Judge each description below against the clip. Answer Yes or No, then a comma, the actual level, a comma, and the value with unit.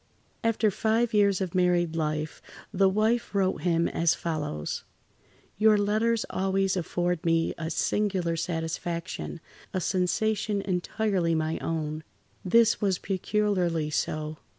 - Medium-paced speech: No, slow, 120 wpm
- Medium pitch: Yes, medium, 180 Hz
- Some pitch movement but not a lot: Yes, average, 3.9 semitones